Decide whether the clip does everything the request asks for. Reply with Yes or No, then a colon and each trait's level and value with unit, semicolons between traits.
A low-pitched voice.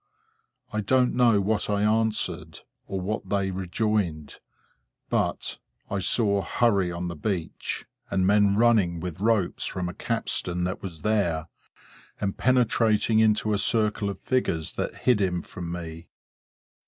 Yes: low, 100 Hz